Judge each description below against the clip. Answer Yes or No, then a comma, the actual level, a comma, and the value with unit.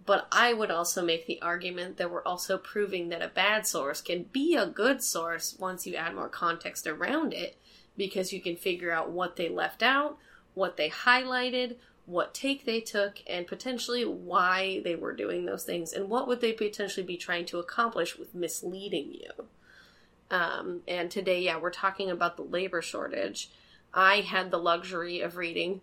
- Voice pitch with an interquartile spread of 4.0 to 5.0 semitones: Yes, average, 4.7 semitones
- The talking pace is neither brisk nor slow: Yes, average, 185 wpm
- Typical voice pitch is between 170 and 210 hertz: Yes, high, 190 Hz